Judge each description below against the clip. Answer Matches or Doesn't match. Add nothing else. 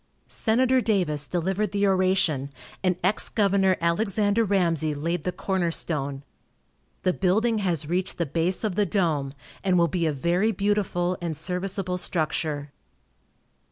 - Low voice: Doesn't match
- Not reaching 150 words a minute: Matches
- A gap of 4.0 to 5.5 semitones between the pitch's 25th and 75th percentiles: Doesn't match